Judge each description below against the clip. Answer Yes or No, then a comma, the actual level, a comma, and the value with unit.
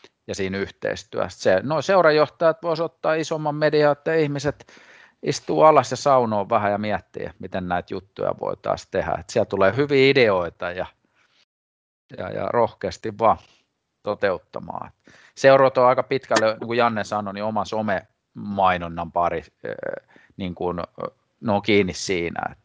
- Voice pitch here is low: Yes, low, 110 Hz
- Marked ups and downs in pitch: Yes, wide, 7.0 semitones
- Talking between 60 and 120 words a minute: No, average, 135 wpm